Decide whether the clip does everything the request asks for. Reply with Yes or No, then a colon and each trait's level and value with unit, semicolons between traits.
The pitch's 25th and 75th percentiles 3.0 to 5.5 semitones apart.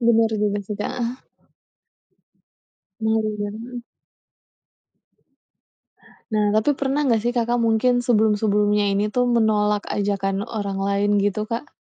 No: narrow, 2.4 semitones